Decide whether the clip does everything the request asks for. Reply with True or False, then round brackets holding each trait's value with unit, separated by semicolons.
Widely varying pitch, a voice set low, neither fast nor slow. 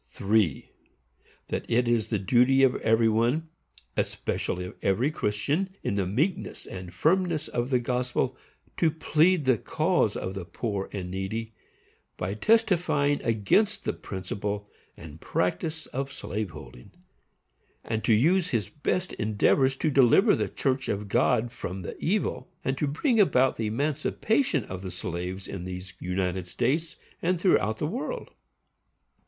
True (7.6 semitones; 120 Hz; 150 wpm)